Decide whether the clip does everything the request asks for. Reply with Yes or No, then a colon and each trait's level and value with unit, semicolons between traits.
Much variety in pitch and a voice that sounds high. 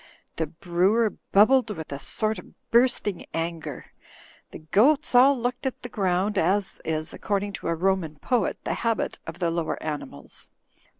Yes: wide, 5.9 semitones; high, 195 Hz